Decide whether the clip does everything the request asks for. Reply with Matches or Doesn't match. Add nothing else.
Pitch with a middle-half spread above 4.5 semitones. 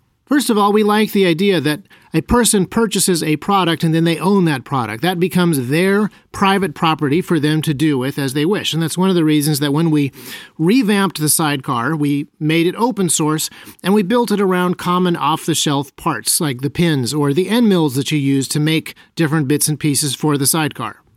Doesn't match